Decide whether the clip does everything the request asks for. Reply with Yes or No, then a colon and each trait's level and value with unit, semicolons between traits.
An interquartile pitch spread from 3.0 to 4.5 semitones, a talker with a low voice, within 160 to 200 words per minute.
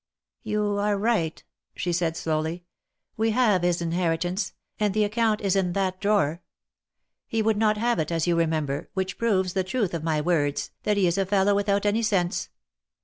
No: average, 3.7 semitones; high, 190 Hz; average, 190 wpm